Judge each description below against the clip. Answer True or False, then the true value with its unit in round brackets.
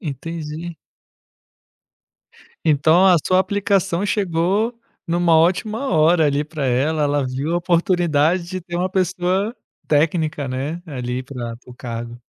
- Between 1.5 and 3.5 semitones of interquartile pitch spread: False (4.1 semitones)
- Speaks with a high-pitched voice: False (165 Hz)